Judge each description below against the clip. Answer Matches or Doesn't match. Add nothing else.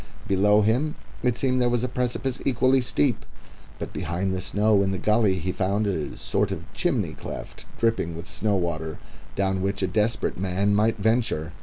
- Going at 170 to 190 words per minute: Matches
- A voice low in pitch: Matches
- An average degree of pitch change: Matches